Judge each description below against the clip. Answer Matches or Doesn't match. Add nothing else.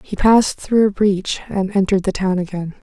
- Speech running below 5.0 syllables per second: Doesn't match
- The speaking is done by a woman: Matches